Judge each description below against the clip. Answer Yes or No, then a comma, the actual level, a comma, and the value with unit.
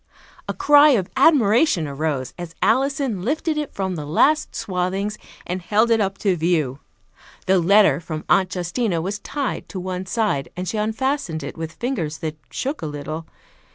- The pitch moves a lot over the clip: Yes, wide, 6.0 semitones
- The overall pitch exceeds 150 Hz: Yes, high, 190 Hz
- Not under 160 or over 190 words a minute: Yes, average, 170 wpm